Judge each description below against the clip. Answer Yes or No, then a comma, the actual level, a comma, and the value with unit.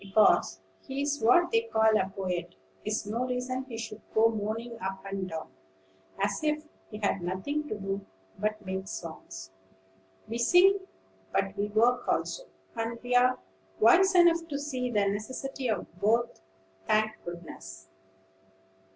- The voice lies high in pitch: Yes, high, 220 Hz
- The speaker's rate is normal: Yes, average, 145 wpm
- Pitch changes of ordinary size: Yes, average, 4.6 semitones